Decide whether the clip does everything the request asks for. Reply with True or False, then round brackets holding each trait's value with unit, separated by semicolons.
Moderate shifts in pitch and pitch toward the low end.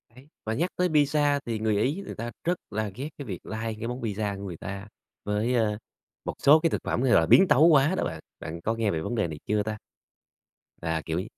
False (5.7 semitones; 110 Hz)